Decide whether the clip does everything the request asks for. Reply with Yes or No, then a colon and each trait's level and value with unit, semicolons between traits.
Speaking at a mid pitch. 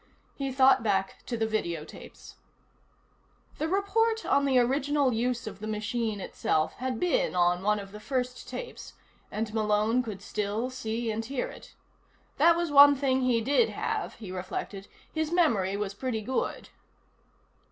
No: high, 235 Hz